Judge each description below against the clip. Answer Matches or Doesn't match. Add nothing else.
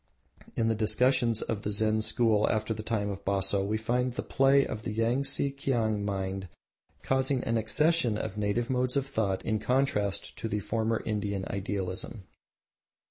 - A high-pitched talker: Doesn't match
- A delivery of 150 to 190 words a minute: Matches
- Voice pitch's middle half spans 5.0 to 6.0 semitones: Doesn't match